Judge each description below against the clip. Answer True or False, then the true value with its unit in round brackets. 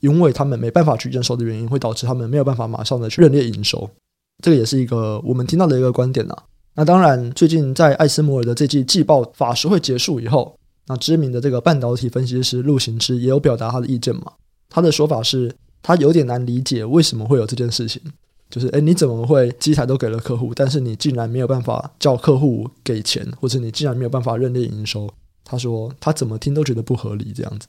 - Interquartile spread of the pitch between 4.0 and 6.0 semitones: False (3.6 semitones)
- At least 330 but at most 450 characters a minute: True (365 characters per minute)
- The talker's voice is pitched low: True (125 Hz)